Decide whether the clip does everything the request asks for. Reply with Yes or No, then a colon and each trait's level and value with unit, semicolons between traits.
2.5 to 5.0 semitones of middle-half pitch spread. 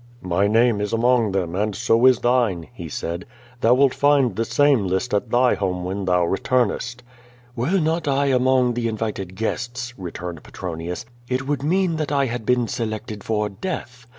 Yes: average, 4.5 semitones